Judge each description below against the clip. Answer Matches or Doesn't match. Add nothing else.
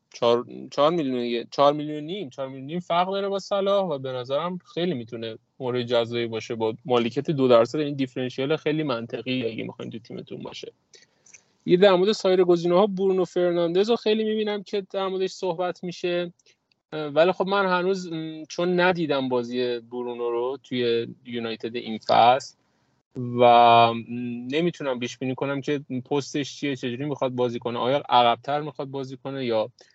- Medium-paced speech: Doesn't match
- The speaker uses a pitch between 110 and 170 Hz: Matches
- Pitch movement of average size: Doesn't match